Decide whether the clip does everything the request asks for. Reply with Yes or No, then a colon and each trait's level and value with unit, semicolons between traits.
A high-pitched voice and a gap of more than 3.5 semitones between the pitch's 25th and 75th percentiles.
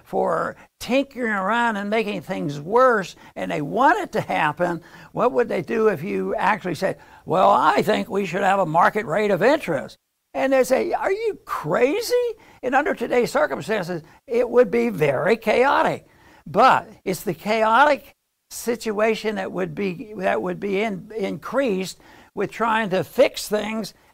Yes: high, 215 Hz; average, 3.9 semitones